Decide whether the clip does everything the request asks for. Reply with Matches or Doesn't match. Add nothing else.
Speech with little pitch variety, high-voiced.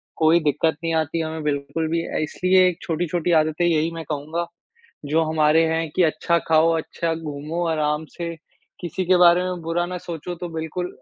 Doesn't match